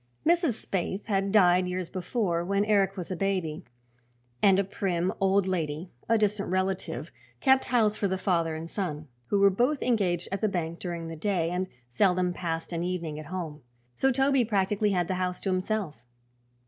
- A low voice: No, medium, 185 Hz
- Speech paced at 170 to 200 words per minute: Yes, average, 185 wpm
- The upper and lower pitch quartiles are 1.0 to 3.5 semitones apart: Yes, average, 2.8 semitones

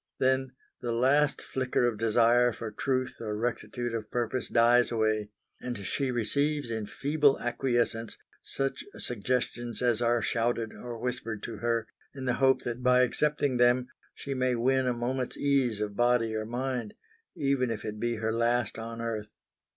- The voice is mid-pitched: No, low, 120 Hz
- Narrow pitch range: Yes, narrow, 2.0 semitones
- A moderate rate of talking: Yes, average, 165 wpm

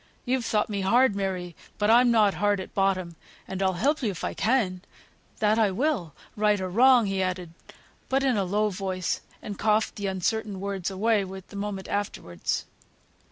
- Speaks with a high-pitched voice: Yes, high, 200 Hz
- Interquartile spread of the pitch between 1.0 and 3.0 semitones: Yes, average, 2.7 semitones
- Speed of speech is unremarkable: Yes, average, 180 wpm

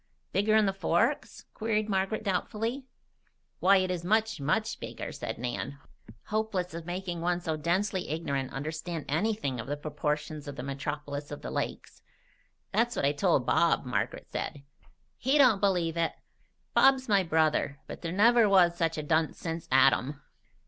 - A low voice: No, medium, 170 Hz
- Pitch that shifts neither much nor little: No, wide, 5.8 semitones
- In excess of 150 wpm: Yes, average, 160 wpm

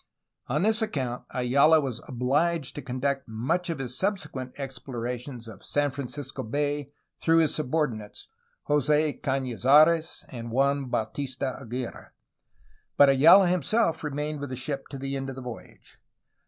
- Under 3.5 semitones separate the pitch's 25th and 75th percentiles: Yes, average, 3.1 semitones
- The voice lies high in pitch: No, medium, 140 Hz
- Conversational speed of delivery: Yes, average, 150 wpm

